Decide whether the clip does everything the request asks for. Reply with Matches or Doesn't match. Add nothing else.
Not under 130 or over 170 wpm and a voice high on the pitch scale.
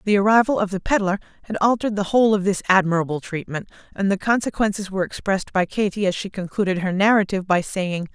Doesn't match